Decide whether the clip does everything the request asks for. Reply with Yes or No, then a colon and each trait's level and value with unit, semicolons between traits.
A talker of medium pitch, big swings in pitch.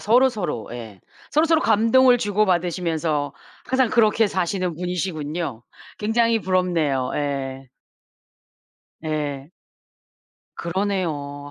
Yes: medium, 175 Hz; wide, 6.6 semitones